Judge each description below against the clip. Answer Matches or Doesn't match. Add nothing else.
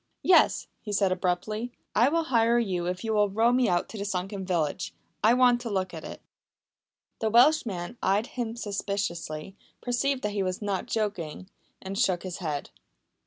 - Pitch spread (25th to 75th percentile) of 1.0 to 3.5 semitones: Doesn't match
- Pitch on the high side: Matches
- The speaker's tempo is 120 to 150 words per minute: Doesn't match